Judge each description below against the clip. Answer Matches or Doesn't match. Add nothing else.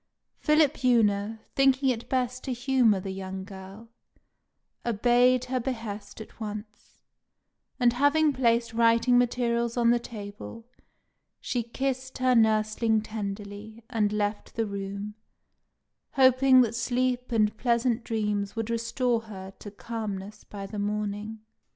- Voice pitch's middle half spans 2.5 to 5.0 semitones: Matches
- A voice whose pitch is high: Matches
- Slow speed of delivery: Matches